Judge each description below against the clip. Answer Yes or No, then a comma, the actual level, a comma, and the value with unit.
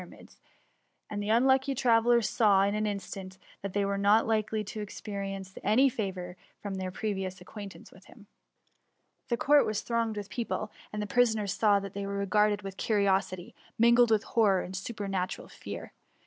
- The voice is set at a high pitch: Yes, high, 205 Hz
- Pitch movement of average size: No, narrow, 2.3 semitones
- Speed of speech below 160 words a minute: No, average, 190 wpm